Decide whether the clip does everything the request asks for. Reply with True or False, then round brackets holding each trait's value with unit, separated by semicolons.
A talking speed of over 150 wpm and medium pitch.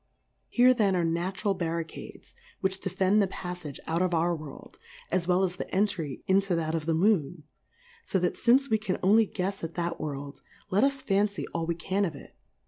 True (190 wpm; 180 Hz)